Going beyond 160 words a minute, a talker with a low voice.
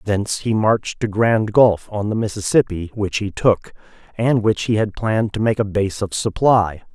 Yes: average, 200 wpm; low, 105 Hz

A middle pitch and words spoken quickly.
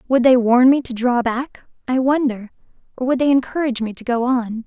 No: very high, 250 Hz; fast, 220 wpm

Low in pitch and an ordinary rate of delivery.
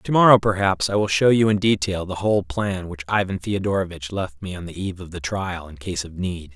No: very low, 95 Hz; fast, 245 wpm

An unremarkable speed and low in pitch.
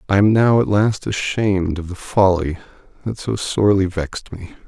Yes: average, 180 wpm; very low, 95 Hz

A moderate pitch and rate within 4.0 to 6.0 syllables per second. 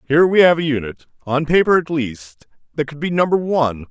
Yes: medium, 145 Hz; 5.8 syllables/s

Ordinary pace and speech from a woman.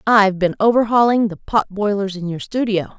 Yes: average, 180 wpm; female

